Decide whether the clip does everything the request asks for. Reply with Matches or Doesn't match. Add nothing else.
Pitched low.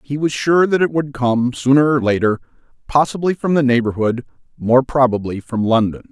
Matches